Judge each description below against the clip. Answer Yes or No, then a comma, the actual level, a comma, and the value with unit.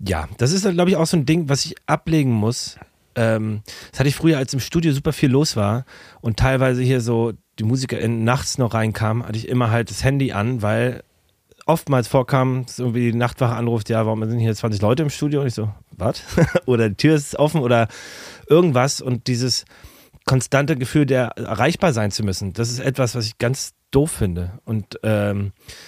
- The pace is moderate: No, fast, 200 wpm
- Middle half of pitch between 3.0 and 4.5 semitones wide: Yes, average, 3.7 semitones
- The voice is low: Yes, low, 125 Hz